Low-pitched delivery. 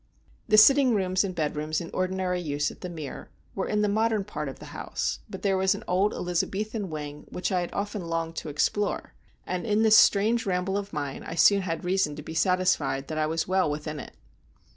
No: medium, 180 Hz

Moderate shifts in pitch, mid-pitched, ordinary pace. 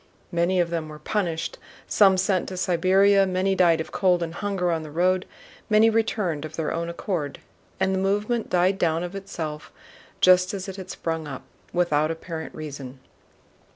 Yes: average, 3.0 semitones; medium, 180 Hz; average, 175 wpm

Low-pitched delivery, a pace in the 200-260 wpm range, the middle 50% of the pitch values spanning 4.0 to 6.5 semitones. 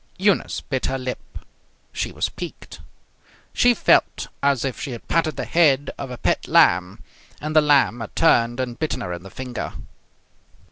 No: low, 130 Hz; average, 175 wpm; average, 4.4 semitones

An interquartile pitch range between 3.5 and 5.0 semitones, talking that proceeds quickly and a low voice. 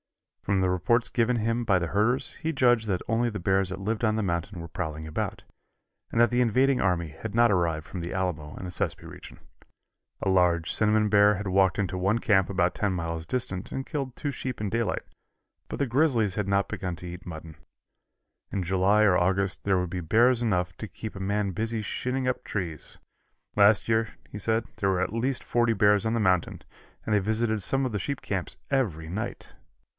Yes: average, 4.0 semitones; fast, 210 wpm; low, 100 Hz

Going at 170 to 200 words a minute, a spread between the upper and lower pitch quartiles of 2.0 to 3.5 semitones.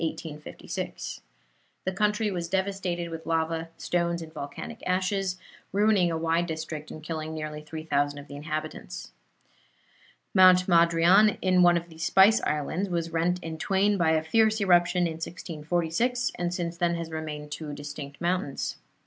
No: average, 150 wpm; average, 2.7 semitones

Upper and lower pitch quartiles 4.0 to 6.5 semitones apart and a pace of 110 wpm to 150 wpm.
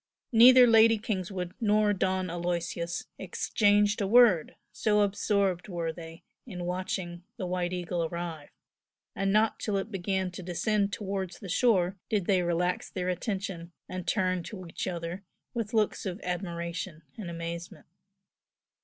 No: average, 2.9 semitones; average, 145 wpm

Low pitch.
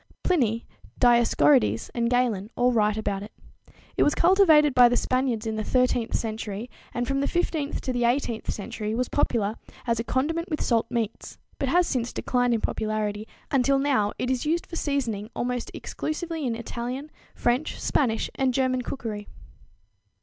No: high, 245 Hz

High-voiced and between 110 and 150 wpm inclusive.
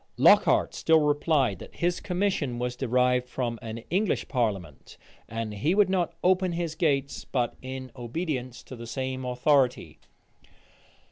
No: low, 130 Hz; average, 140 wpm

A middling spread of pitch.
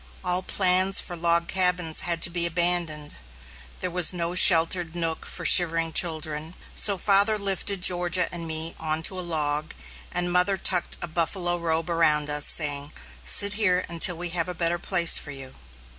No: narrow, 2.0 semitones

